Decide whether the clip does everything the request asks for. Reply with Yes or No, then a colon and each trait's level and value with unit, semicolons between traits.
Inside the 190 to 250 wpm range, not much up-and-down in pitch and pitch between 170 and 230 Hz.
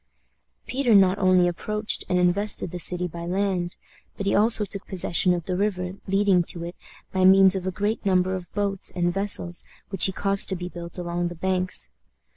Yes: average, 195 wpm; narrow, 2.0 semitones; medium, 185 Hz